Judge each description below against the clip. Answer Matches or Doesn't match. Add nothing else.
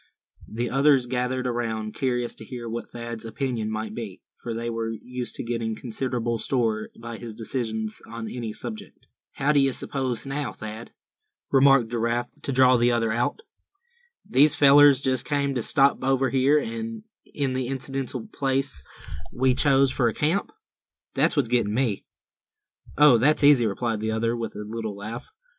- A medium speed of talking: Matches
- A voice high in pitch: Doesn't match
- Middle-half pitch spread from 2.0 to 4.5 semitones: Matches